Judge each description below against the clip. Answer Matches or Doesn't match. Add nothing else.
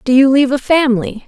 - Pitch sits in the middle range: Doesn't match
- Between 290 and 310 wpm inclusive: Doesn't match